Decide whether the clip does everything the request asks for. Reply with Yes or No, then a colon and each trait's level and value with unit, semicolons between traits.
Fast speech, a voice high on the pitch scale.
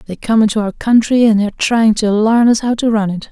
Yes: fast, 270 wpm; high, 220 Hz